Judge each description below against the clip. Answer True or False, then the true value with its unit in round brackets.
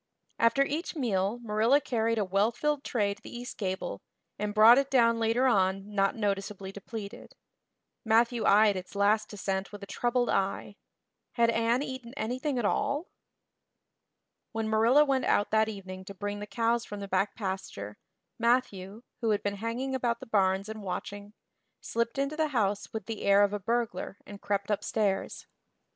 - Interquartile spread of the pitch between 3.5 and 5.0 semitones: False (3.1 semitones)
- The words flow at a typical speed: True (170 wpm)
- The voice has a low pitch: False (220 Hz)